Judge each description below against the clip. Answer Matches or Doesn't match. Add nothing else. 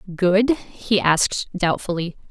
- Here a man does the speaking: Doesn't match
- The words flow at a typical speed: Doesn't match